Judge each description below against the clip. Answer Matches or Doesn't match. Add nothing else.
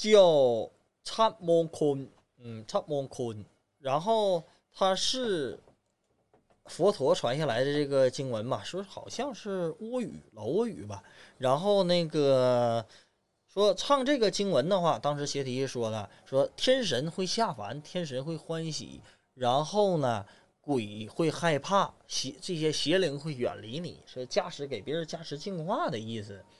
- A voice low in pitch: Doesn't match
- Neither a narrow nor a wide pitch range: Doesn't match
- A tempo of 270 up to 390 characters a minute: Doesn't match